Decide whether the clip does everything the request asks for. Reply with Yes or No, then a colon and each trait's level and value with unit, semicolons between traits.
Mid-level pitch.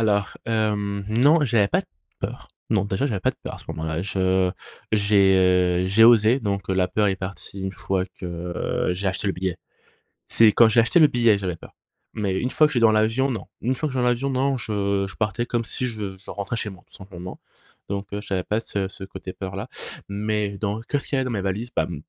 No: low, 100 Hz